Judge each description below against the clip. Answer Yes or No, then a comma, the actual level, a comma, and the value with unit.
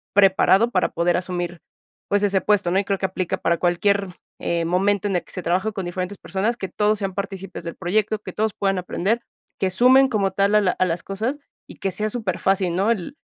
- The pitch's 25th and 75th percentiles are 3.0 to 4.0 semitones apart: No, narrow, 2.4 semitones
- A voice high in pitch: Yes, high, 195 Hz